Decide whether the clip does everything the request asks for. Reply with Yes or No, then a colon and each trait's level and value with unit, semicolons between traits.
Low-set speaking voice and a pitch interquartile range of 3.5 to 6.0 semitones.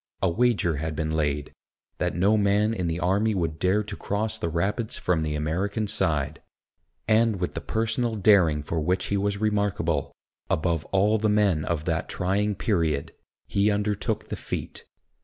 Yes: very low, 95 Hz; average, 4.5 semitones